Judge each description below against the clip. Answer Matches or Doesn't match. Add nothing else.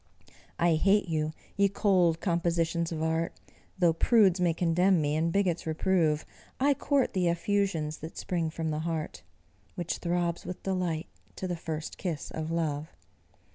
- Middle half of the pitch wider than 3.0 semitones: Doesn't match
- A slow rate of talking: Doesn't match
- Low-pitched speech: Doesn't match